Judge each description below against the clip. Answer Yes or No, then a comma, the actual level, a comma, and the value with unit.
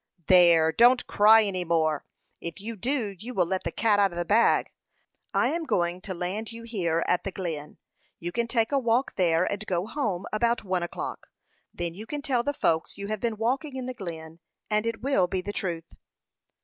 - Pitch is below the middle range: No, high, 200 Hz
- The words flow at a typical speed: No, fast, 210 wpm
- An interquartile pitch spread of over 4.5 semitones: Yes, average, 5.0 semitones